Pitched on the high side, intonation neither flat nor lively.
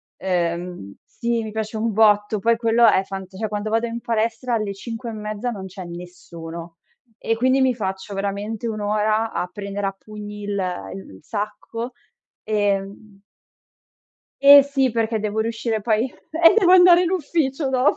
Yes: high, 215 Hz; average, 3.0 semitones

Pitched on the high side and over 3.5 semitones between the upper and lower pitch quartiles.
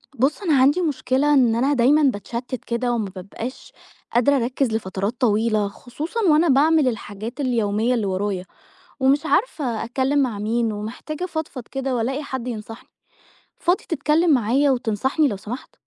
Yes: very high, 255 Hz; average, 4.3 semitones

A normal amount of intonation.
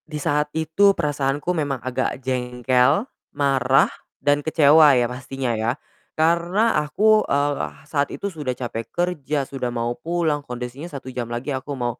Yes: average, 3.9 semitones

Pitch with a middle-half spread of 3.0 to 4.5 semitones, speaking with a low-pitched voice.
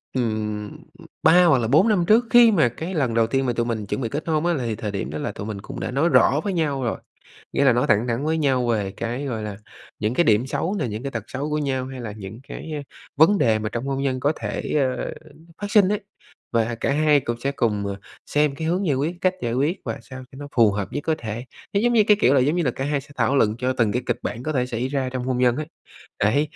No: average, 4.9 semitones; low, 130 Hz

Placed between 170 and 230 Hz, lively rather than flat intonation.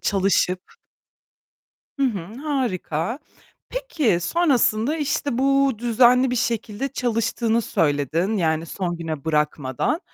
Yes: high, 225 Hz; wide, 7.5 semitones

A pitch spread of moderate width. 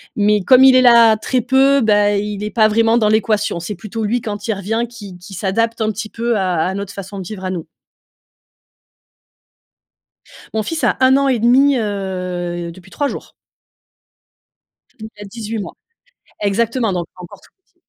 Yes: average, 3.1 semitones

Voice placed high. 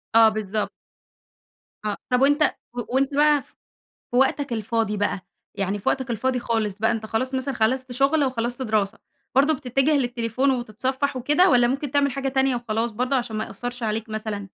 Yes: high, 245 Hz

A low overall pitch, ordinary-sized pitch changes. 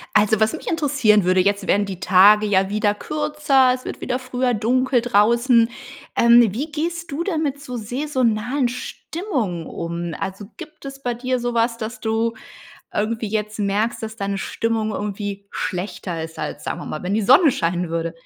No: high, 225 Hz; average, 4.2 semitones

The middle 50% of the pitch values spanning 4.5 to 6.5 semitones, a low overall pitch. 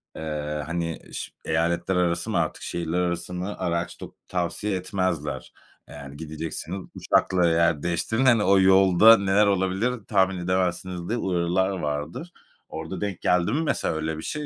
No: narrow, 2.6 semitones; very low, 90 Hz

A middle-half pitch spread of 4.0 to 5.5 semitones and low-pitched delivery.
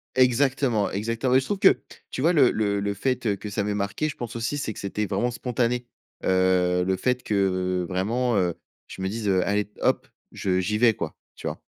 Yes: average, 4.3 semitones; low, 105 Hz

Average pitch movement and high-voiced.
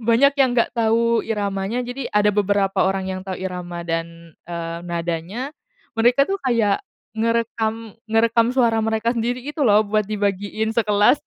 Yes: average, 3.2 semitones; high, 220 Hz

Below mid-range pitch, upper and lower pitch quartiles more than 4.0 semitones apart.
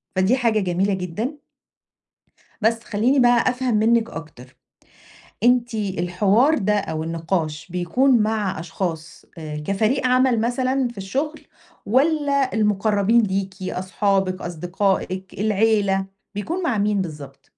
No: high, 205 Hz; average, 4.7 semitones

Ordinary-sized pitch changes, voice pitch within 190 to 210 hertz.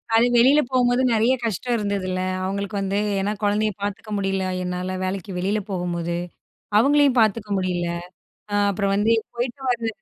Yes: average, 3.7 semitones; high, 205 Hz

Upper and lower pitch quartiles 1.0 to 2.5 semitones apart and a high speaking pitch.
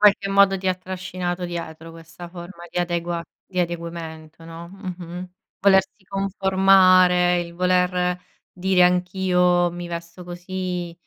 No: narrow, 1.4 semitones; medium, 180 Hz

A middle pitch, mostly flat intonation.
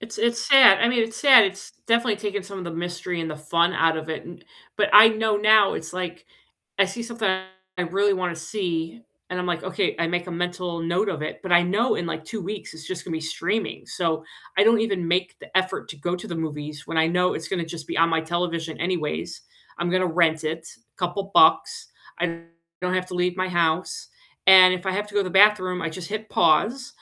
No: medium, 180 Hz; average, 3.5 semitones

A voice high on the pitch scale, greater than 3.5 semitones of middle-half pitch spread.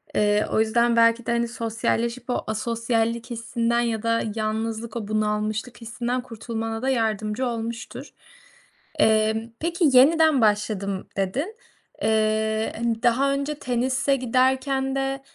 No: high, 230 Hz; narrow, 2.5 semitones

